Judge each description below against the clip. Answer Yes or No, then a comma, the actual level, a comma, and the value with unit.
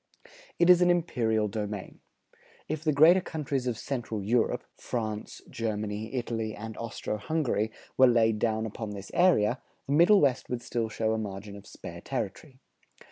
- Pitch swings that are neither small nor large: Yes, average, 4.6 semitones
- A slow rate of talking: No, average, 160 wpm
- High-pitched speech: No, low, 115 Hz